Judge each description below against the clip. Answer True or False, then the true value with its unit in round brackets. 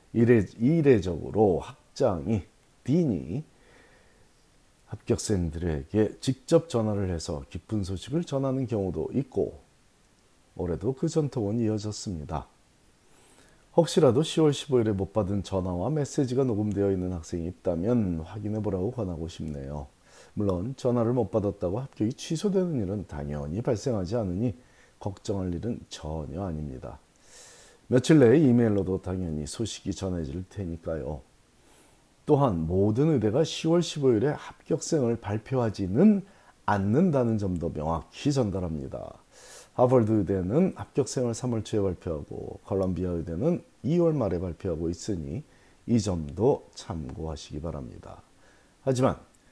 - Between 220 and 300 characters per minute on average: True (285 characters per minute)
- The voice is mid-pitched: False (105 Hz)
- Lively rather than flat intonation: True (6.2 semitones)